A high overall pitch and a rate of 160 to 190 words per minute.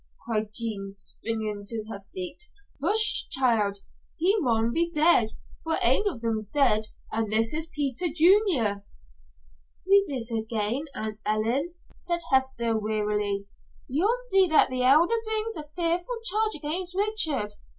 No: very high, 260 Hz; average, 140 wpm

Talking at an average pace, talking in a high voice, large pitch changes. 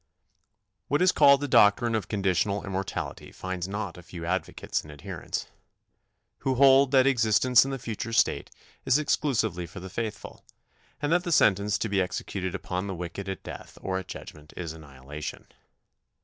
No: average, 165 wpm; low, 100 Hz; wide, 5.8 semitones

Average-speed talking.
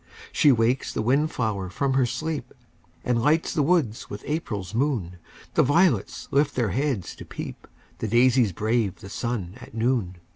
Yes: average, 170 wpm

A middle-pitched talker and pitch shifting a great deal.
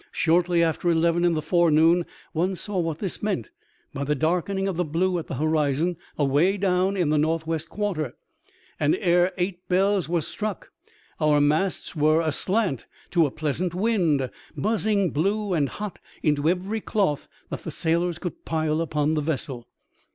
No: medium, 170 Hz; average, 3.3 semitones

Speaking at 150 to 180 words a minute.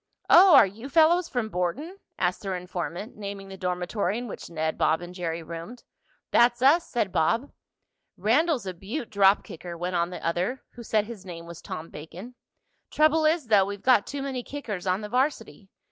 No: average, 190 wpm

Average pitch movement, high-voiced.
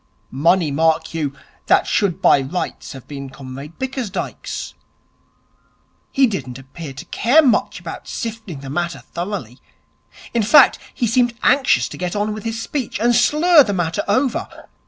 No: wide, 7.3 semitones; high, 195 Hz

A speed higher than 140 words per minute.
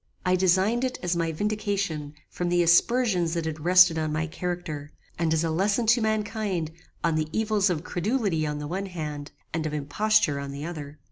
Yes: average, 195 wpm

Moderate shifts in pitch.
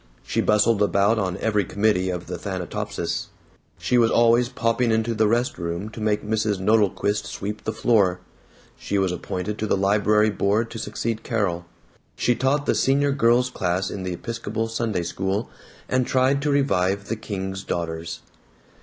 Yes: average, 3.3 semitones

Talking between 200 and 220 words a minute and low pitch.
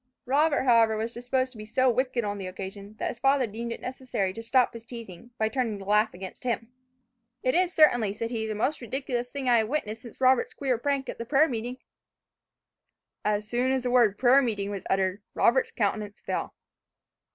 No: fast, 205 wpm; high, 235 Hz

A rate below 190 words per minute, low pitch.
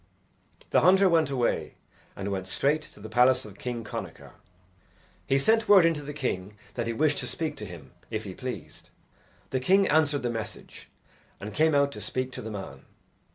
No: average, 195 wpm; low, 130 Hz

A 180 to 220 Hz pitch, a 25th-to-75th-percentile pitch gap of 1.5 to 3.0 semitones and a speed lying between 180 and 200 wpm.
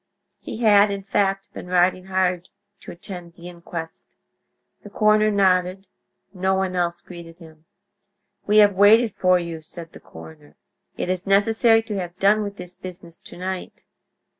No: medium, 185 Hz; narrow, 2.6 semitones; average, 160 wpm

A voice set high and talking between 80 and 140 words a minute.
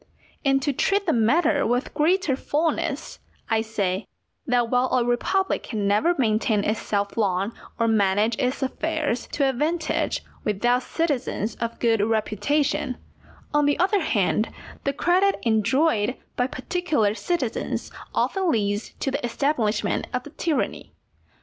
Yes: very high, 250 Hz; slow, 135 wpm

